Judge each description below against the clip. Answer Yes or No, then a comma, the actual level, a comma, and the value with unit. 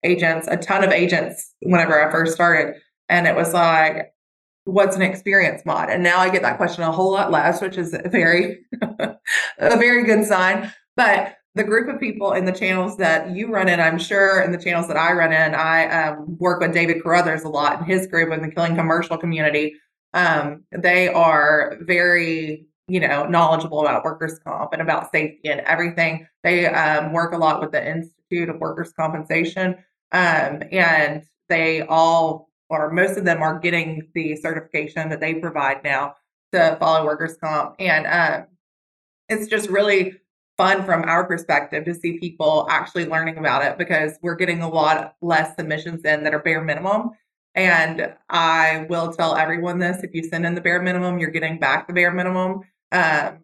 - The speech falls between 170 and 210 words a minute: Yes, average, 185 wpm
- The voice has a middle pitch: Yes, medium, 170 Hz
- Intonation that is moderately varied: No, narrow, 2.3 semitones